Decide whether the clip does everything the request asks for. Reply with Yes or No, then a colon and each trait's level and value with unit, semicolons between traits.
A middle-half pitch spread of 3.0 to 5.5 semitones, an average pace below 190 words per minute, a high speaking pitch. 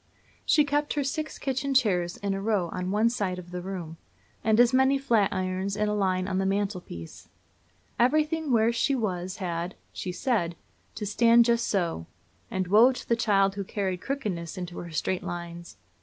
Yes: average, 4.5 semitones; average, 180 wpm; high, 200 Hz